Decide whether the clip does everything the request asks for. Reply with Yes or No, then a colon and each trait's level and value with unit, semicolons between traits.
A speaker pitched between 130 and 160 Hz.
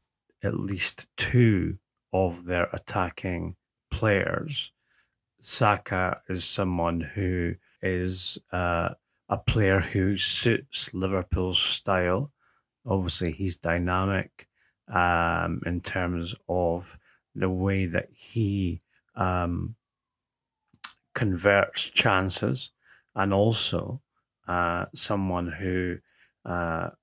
No: very low, 95 Hz